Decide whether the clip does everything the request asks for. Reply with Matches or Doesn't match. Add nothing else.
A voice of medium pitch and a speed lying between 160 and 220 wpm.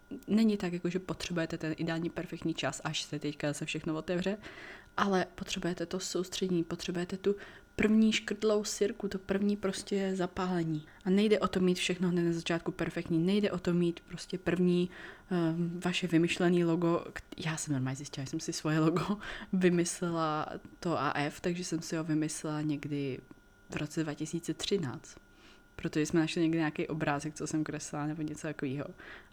Matches